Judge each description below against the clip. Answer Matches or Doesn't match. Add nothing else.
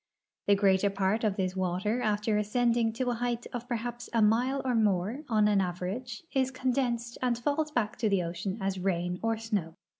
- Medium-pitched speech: Doesn't match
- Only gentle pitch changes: Doesn't match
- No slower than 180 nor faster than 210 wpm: Matches